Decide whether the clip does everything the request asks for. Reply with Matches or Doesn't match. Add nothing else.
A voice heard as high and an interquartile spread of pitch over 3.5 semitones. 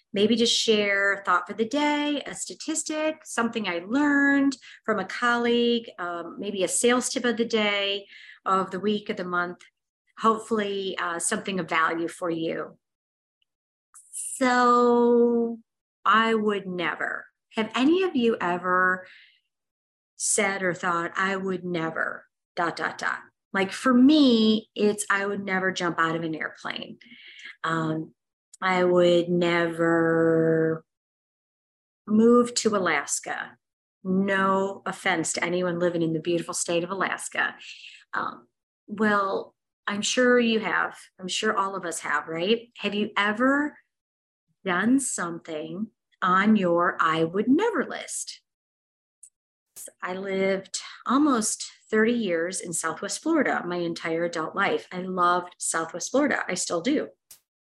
Matches